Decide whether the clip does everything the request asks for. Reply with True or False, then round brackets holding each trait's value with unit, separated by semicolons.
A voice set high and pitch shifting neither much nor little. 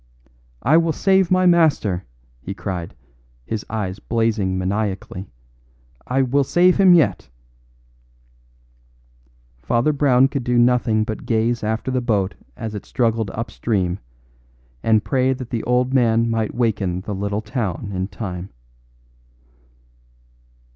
False (115 Hz; 4.1 semitones)